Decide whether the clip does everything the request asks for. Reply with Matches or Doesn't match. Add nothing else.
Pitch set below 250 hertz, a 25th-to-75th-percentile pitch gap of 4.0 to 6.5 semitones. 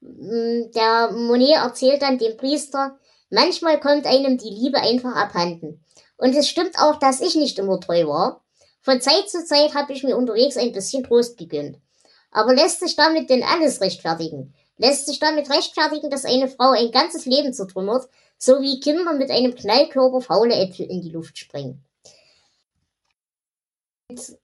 Doesn't match